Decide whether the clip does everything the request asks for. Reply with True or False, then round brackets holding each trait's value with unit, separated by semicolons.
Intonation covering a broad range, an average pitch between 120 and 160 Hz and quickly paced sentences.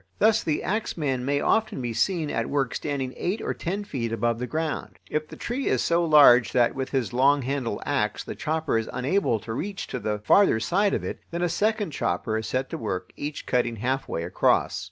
True (6.3 semitones; 140 Hz; 215 wpm)